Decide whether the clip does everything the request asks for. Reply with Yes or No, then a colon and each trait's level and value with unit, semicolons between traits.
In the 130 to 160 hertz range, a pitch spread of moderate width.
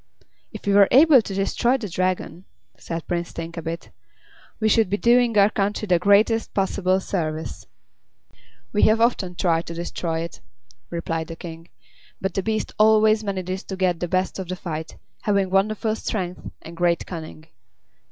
No: high, 190 Hz; average, 3.9 semitones